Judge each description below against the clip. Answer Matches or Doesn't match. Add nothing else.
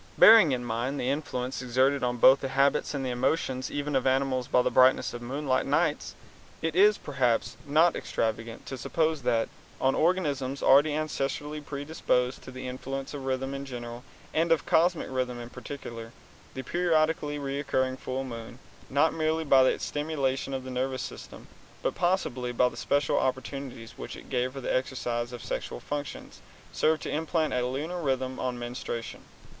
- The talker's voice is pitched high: Doesn't match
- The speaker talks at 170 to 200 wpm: Matches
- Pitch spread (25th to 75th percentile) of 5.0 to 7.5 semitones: Doesn't match